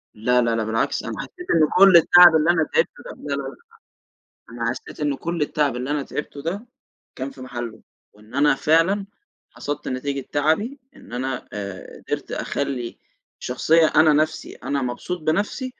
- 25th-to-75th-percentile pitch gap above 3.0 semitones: Yes, average, 5.0 semitones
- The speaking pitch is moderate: Yes, medium, 145 Hz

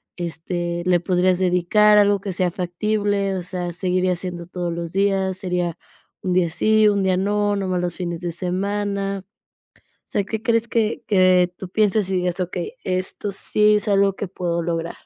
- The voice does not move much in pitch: Yes, narrow, 2.3 semitones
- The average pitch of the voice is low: No, medium, 185 Hz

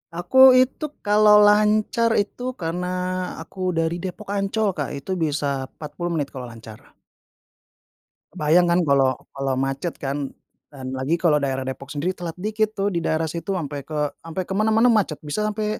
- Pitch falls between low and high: Yes, medium, 170 Hz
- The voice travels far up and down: Yes, wide, 6.5 semitones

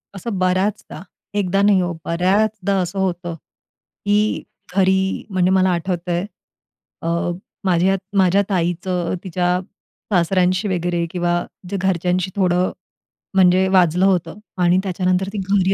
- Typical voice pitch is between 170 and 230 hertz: Yes, medium, 185 Hz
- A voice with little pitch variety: Yes, narrow, 1.5 semitones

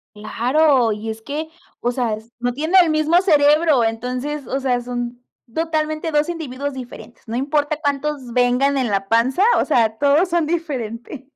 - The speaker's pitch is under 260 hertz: No, very high, 270 Hz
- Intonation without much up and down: No, average, 4.2 semitones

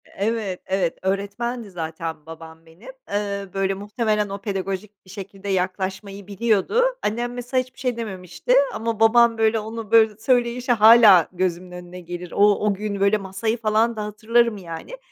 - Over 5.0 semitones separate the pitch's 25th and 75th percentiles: No, average, 3.2 semitones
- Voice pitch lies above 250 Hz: No, high, 205 Hz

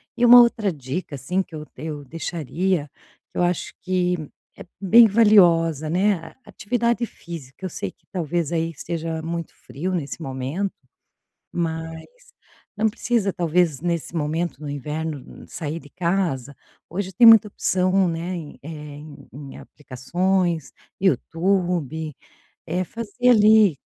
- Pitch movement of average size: Yes, average, 3.8 semitones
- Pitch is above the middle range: No, medium, 170 Hz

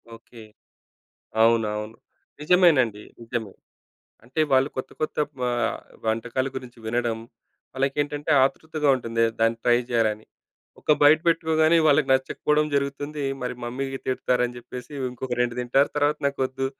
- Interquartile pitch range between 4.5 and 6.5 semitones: No, average, 3.7 semitones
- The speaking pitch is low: Yes, low, 130 Hz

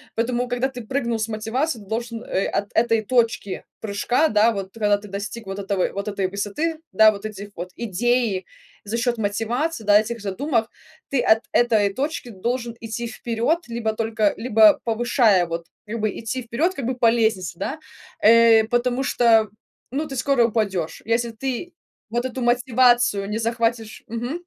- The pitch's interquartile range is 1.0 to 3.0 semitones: Yes, narrow, 2.6 semitones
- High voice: Yes, high, 230 Hz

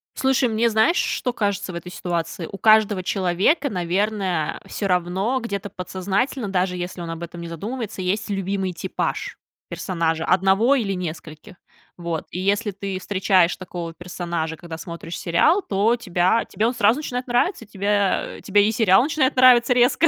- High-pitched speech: Yes, high, 195 Hz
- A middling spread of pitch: Yes, average, 4.0 semitones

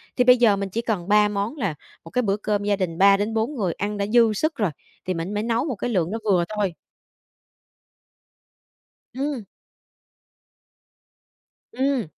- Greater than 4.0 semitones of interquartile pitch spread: No, average, 3.2 semitones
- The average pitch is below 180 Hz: No, high, 210 Hz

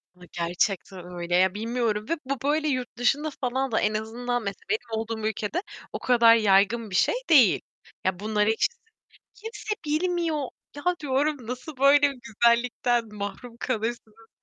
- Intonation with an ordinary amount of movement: Yes, average, 4.5 semitones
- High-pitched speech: Yes, high, 235 Hz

